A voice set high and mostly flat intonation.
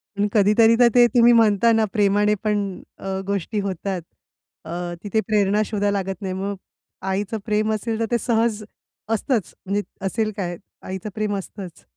Yes: high, 210 Hz; narrow, 2.1 semitones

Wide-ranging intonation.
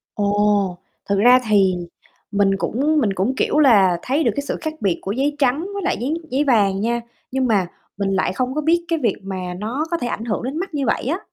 Yes: wide, 6.4 semitones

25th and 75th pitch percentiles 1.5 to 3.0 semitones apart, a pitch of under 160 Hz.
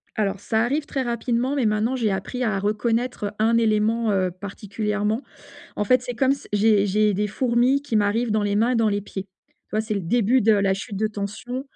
No: average, 2.7 semitones; high, 215 Hz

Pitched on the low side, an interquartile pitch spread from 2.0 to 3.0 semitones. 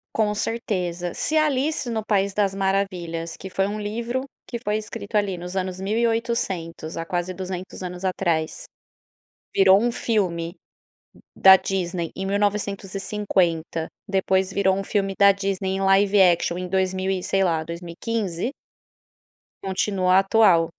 No: high, 195 Hz; narrow, 2.4 semitones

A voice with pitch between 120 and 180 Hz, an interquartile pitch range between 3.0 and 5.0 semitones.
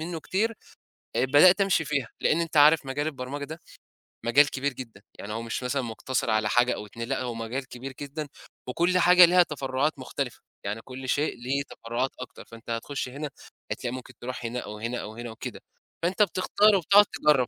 Yes: low, 135 Hz; average, 4.5 semitones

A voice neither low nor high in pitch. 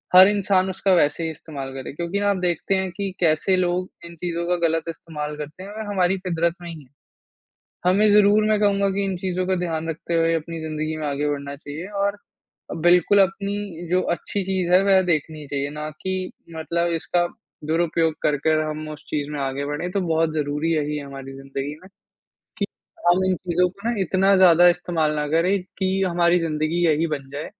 Yes: medium, 170 Hz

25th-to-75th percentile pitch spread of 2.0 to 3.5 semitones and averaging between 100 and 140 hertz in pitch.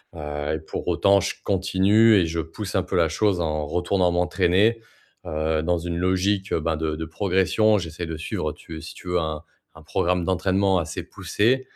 No: average, 3.1 semitones; very low, 90 Hz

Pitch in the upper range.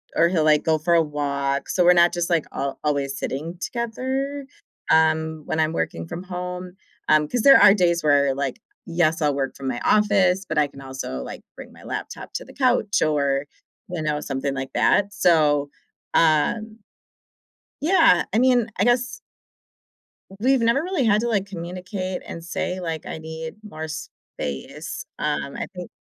No: medium, 165 Hz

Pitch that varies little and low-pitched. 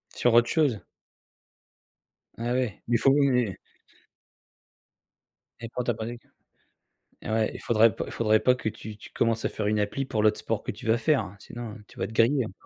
Yes: narrow, 2.3 semitones; low, 115 Hz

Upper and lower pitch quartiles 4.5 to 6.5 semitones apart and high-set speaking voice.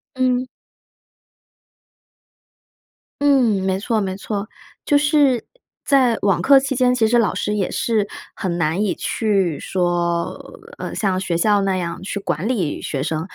Yes: average, 5.2 semitones; high, 205 Hz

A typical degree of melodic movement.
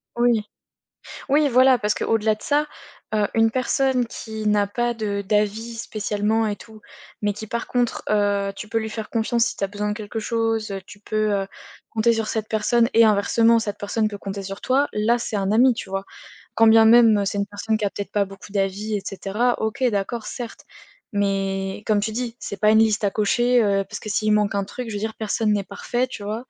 No: narrow, 2.1 semitones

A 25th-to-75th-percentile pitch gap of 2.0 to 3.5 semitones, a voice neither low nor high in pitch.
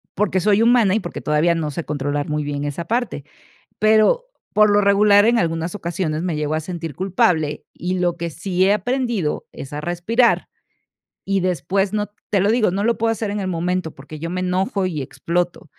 No: average, 4.4 semitones; medium, 180 Hz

